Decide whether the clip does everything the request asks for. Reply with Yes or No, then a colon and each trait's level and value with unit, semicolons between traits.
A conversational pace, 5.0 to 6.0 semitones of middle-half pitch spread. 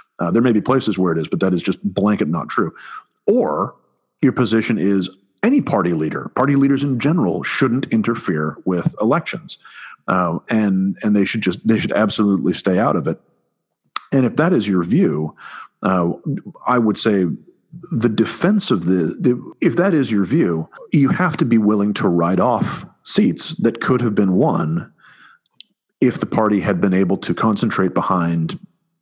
Yes: average, 180 wpm; wide, 5.4 semitones